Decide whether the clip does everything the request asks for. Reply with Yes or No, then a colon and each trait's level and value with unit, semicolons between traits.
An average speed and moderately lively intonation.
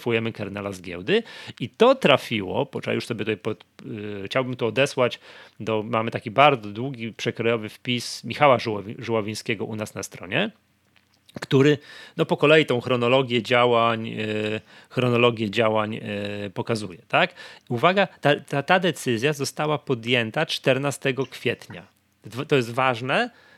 Yes: average, 130 wpm; average, 4.0 semitones